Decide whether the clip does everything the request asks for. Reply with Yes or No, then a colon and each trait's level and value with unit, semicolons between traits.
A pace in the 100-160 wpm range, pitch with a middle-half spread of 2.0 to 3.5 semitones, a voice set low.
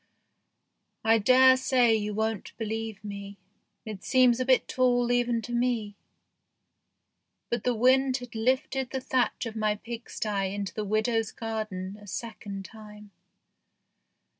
No: slow, 135 wpm; average, 2.9 semitones; high, 225 Hz